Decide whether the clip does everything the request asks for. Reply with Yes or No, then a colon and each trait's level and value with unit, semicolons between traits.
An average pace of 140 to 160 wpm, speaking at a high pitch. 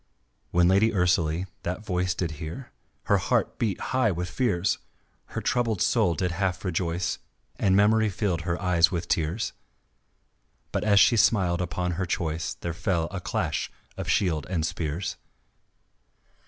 No: average, 150 wpm; very low, 90 Hz